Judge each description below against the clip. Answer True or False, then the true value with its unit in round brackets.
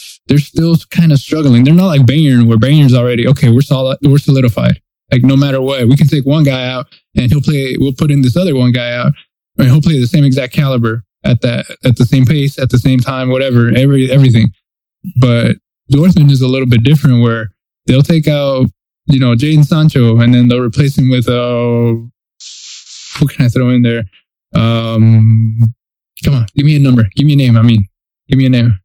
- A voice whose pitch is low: True (130 Hz)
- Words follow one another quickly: True (215 wpm)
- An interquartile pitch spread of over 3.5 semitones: False (2.8 semitones)